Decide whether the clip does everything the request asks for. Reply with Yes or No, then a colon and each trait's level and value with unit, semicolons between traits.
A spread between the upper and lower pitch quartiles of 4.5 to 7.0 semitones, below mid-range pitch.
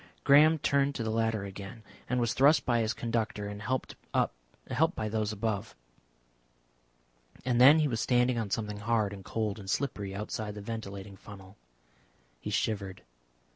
No: average, 3.1 semitones; low, 110 Hz